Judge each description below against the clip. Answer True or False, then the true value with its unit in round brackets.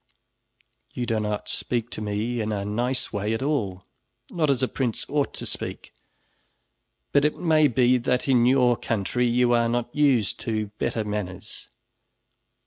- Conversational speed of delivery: True (160 wpm)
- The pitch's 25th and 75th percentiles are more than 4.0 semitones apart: False (3.3 semitones)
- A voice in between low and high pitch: False (120 Hz)